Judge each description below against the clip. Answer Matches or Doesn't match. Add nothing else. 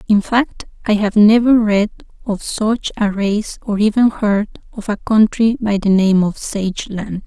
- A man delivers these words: Doesn't match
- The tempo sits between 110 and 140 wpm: Doesn't match